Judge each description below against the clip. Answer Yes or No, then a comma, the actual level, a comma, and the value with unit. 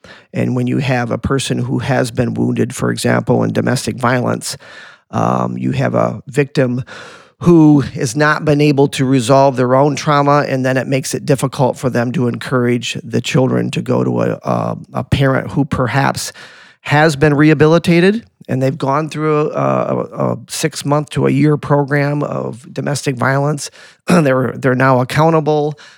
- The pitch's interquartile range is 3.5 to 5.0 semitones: No, average, 3.1 semitones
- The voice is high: No, low, 135 Hz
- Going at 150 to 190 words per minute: Yes, average, 165 wpm